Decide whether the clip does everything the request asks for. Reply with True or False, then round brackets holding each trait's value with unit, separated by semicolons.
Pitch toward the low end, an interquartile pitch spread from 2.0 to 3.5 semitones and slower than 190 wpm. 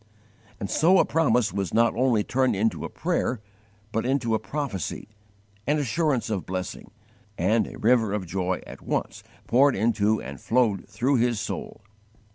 False (115 Hz; 4.1 semitones; 160 wpm)